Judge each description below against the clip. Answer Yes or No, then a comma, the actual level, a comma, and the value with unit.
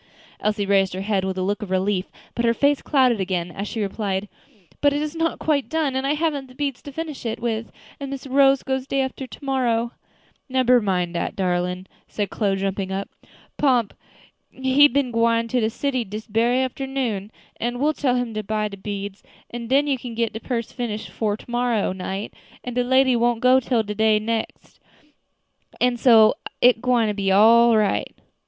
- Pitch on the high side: Yes, high, 235 Hz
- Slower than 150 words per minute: No, average, 200 wpm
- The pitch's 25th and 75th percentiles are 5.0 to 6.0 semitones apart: No, average, 4.1 semitones